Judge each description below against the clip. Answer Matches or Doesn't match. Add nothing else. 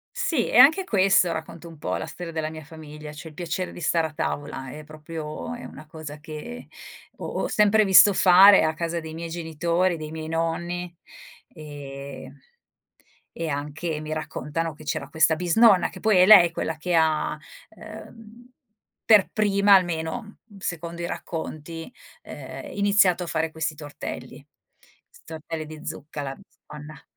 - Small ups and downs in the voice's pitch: Doesn't match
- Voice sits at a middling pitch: Matches